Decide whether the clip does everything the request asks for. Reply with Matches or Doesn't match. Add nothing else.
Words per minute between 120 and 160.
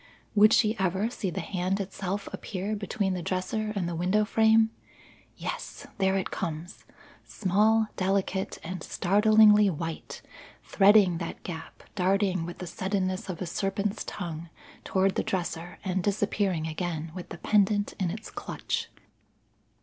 Matches